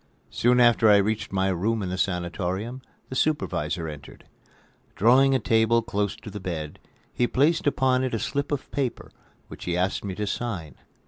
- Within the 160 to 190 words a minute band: Yes, average, 180 wpm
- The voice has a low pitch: Yes, low, 105 Hz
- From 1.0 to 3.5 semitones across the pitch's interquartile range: No, average, 5.2 semitones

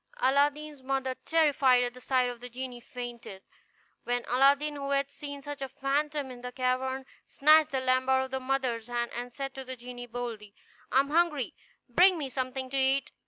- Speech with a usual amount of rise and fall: No, narrow, 2.1 semitones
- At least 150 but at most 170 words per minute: No, average, 195 wpm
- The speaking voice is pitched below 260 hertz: No, very high, 265 Hz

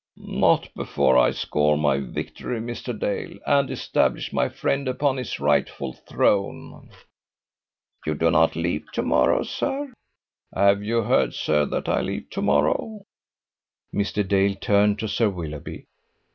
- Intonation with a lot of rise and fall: Yes, wide, 7.4 semitones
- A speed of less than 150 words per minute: Yes, average, 140 wpm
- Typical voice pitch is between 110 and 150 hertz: No, low, 100 Hz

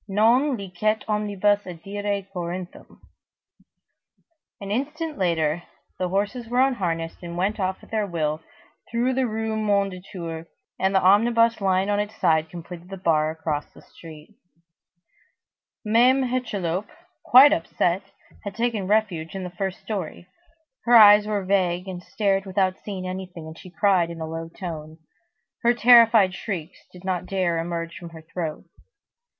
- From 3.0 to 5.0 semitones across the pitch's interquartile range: Yes, average, 3.8 semitones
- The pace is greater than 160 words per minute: No, average, 150 wpm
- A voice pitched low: No, high, 190 Hz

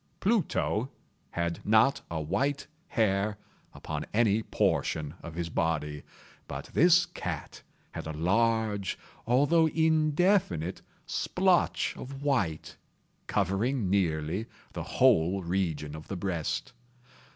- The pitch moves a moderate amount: No, wide, 8.5 semitones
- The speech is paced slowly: Yes, slow, 105 wpm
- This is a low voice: Yes, low, 100 Hz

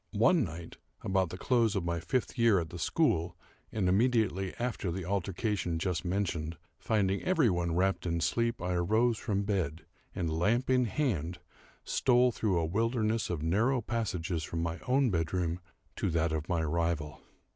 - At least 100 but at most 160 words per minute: No, average, 170 wpm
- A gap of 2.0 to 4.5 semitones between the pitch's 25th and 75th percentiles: No, average, 5.3 semitones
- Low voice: Yes, very low, 95 Hz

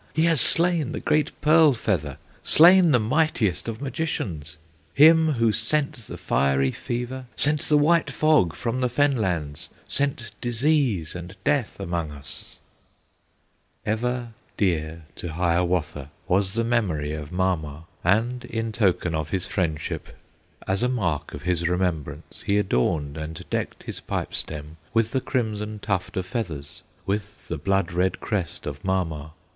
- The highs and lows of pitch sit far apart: Yes, wide, 7.6 semitones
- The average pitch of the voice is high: No, low, 100 Hz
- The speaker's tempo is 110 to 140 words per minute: No, average, 150 wpm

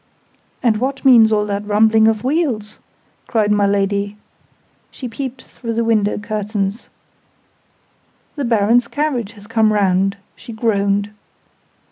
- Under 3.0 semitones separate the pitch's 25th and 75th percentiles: Yes, narrow, 2.4 semitones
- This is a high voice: Yes, high, 215 Hz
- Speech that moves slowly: Yes, slow, 125 wpm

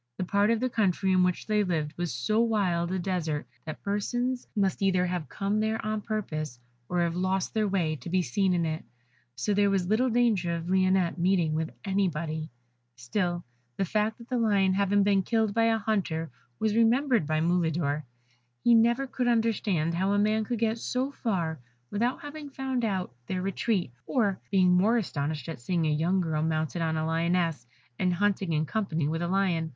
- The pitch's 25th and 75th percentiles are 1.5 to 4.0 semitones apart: No, average, 4.5 semitones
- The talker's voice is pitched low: No, high, 190 Hz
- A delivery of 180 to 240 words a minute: Yes, average, 195 wpm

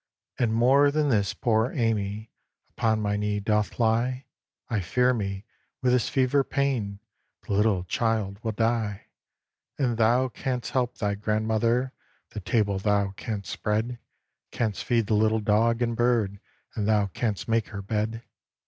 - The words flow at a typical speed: Yes, average, 150 wpm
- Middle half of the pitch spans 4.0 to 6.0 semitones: No, average, 2.7 semitones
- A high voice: No, low, 110 Hz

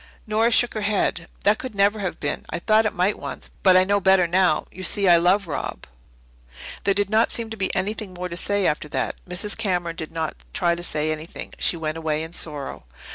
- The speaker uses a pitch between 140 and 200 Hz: Yes, medium, 185 Hz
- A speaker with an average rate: No, fast, 225 wpm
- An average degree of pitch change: Yes, average, 3.5 semitones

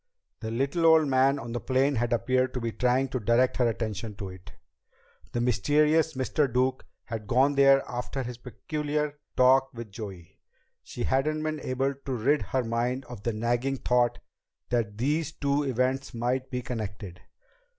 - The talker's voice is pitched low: Yes, low, 130 Hz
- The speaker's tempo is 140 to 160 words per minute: No, average, 170 wpm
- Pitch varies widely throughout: No, average, 2.7 semitones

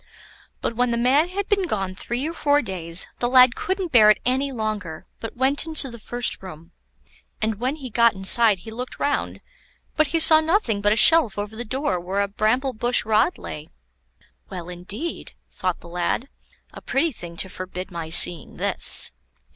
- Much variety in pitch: Yes, wide, 6.2 semitones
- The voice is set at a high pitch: Yes, high, 230 Hz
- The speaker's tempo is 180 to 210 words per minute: Yes, average, 185 wpm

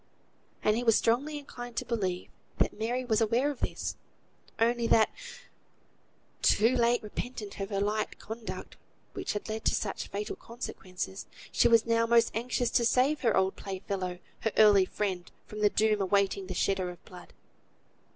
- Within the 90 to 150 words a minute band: No, average, 170 wpm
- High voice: Yes, high, 220 Hz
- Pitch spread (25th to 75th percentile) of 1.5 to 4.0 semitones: Yes, average, 3.1 semitones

